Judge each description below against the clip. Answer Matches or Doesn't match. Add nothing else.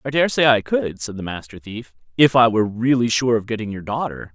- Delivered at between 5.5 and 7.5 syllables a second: Matches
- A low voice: Matches